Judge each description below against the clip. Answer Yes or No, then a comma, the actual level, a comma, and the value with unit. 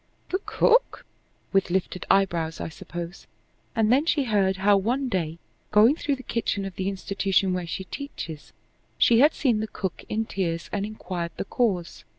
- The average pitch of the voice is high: Yes, high, 195 Hz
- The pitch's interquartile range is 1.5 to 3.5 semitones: No, average, 4.3 semitones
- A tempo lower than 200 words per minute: Yes, average, 170 wpm